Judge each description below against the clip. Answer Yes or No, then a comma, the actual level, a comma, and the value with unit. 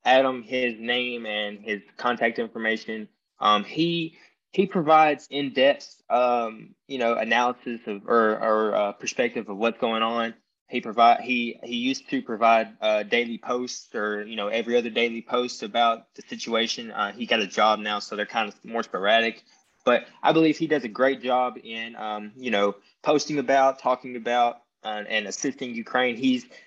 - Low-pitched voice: Yes, low, 120 Hz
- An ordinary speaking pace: Yes, average, 175 wpm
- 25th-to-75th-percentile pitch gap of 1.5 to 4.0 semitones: Yes, average, 3.0 semitones